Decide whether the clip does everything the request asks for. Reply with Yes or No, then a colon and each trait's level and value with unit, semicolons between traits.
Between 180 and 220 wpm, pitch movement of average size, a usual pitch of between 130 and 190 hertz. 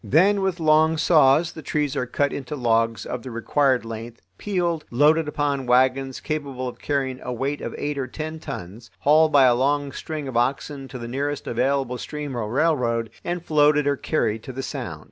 Yes: average, 195 wpm; average, 3.4 semitones; medium, 140 Hz